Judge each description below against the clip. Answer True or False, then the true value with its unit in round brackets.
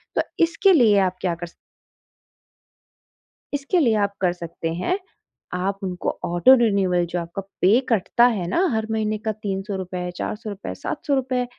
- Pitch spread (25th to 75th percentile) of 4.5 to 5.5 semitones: True (5.0 semitones)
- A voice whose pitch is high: True (200 Hz)